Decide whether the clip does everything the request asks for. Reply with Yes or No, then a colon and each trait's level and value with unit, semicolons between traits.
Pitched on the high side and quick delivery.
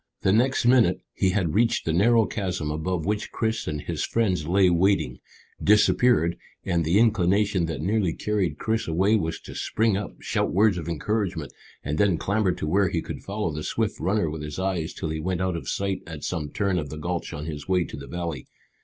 No: very low, 95 Hz; fast, 210 wpm